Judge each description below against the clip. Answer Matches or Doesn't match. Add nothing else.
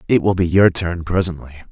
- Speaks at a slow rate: Doesn't match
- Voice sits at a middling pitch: Doesn't match